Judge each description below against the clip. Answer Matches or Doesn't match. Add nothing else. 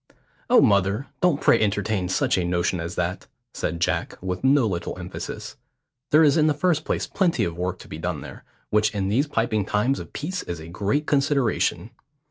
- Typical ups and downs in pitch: Doesn't match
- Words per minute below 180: Doesn't match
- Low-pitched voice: Matches